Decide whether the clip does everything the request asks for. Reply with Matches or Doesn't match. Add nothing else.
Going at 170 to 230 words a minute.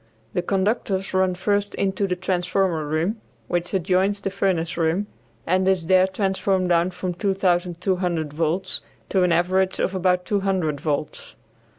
Doesn't match